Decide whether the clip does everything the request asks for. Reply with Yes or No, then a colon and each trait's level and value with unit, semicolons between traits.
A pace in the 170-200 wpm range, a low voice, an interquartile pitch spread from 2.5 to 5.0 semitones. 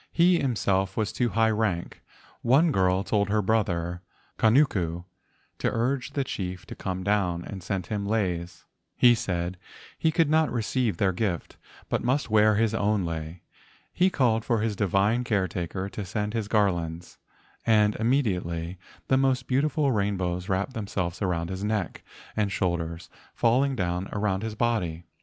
No: average, 160 wpm; low, 105 Hz; average, 4.1 semitones